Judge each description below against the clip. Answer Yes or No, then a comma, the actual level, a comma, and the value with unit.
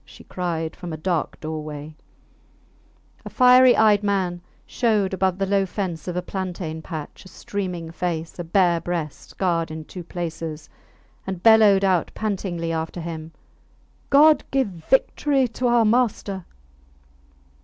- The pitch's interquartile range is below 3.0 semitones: No, average, 3.7 semitones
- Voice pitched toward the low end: No, medium, 180 Hz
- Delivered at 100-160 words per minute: Yes, average, 140 wpm